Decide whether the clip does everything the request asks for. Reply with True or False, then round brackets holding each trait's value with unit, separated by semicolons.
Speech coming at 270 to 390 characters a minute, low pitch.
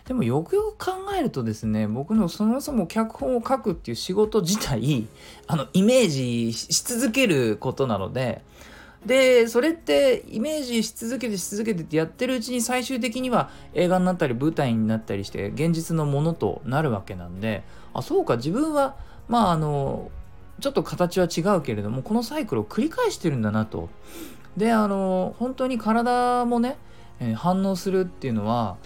False (345 characters per minute; 190 Hz)